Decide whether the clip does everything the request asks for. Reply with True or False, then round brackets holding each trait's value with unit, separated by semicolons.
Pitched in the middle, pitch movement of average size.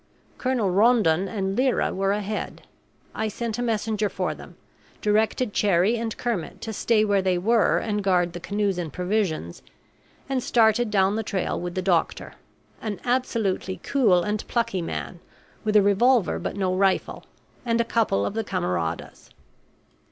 False (205 Hz; 3.4 semitones)